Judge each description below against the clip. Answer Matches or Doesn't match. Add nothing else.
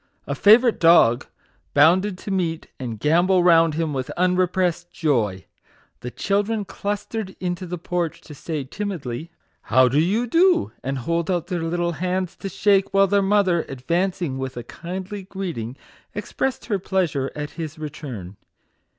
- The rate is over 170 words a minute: Doesn't match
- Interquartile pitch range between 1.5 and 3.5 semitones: Doesn't match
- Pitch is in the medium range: Matches